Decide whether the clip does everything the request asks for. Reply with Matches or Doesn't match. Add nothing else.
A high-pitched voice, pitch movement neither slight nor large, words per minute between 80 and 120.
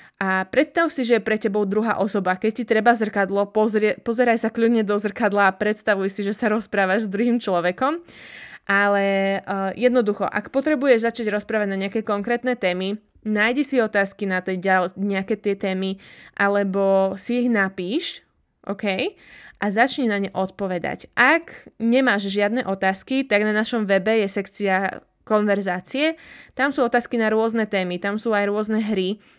Doesn't match